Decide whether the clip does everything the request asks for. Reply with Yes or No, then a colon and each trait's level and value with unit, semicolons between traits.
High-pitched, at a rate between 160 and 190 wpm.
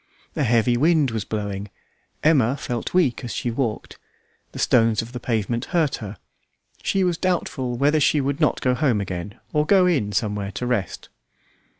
No: low, 125 Hz; average, 175 wpm